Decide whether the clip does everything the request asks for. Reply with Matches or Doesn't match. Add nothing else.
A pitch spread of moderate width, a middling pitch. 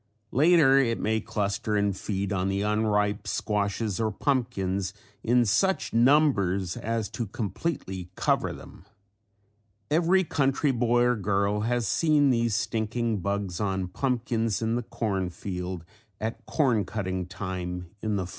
Doesn't match